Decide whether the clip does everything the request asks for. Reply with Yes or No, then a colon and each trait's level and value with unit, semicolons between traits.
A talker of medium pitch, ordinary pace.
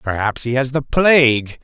No: low, 130 Hz; average, 185 wpm